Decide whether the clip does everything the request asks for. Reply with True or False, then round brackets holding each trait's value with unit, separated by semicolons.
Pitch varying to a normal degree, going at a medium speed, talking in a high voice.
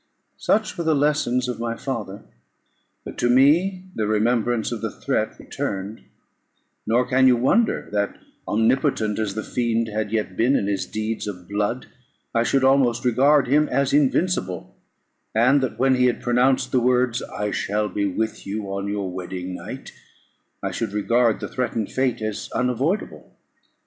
False (3.8 semitones; 165 wpm; 120 Hz)